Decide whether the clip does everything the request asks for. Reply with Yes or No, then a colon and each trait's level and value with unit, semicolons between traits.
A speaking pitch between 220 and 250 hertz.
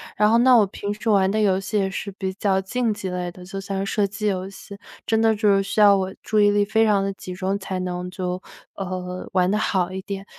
No: high, 195 Hz